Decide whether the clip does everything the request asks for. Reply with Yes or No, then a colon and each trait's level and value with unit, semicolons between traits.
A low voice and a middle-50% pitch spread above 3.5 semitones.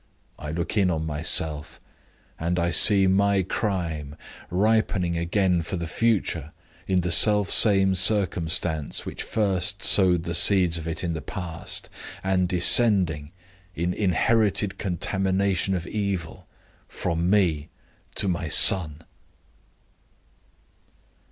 No: very low, 90 Hz; average, 3.0 semitones